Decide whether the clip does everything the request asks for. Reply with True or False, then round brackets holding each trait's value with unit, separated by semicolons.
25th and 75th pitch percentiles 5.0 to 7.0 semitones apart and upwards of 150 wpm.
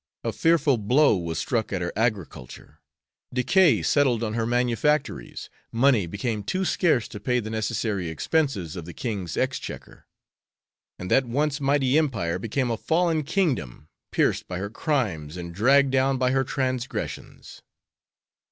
False (5.6 semitones; 145 wpm)